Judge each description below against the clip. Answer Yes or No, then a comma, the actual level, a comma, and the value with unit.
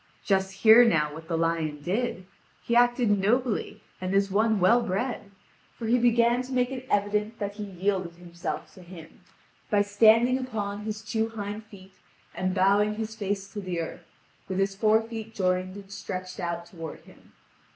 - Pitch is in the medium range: No, high, 205 Hz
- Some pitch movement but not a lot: Yes, average, 3.3 semitones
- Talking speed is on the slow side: No, average, 175 wpm